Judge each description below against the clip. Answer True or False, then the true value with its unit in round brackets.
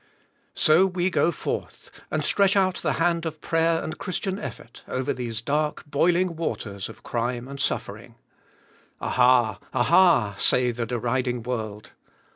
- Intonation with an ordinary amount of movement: False (6.1 semitones)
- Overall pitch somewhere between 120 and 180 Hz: True (135 Hz)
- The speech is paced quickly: False (140 wpm)